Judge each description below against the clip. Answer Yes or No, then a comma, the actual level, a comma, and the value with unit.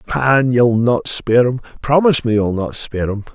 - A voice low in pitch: Yes, low, 120 Hz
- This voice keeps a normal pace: Yes, average, 160 wpm